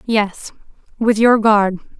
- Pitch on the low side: No, high, 215 Hz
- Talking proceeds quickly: No, slow, 120 wpm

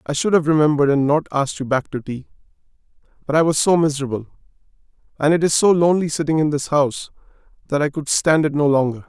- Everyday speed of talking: No, fast, 210 wpm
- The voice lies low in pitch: No, medium, 150 Hz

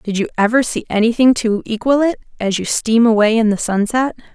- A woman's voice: Yes, female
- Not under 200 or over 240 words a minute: Yes, fast, 205 wpm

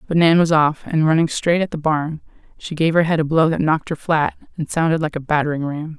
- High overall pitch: No, medium, 160 Hz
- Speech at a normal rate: No, fast, 260 wpm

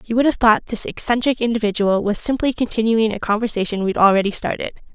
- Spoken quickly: No, average, 180 wpm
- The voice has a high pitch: Yes, high, 220 Hz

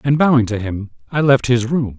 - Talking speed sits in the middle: No, fast, 240 wpm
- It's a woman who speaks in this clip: No, male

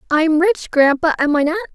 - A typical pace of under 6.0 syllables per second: No, 6.1 syllables/s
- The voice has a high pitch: Yes, very high, 315 Hz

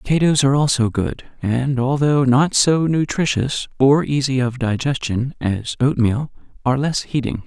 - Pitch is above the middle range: No, low, 135 Hz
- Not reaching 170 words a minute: Yes, average, 145 wpm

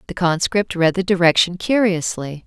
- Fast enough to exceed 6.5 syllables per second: No, 4.8 syllables/s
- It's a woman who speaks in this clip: Yes, female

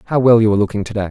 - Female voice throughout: No, male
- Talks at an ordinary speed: No, fast, 380 wpm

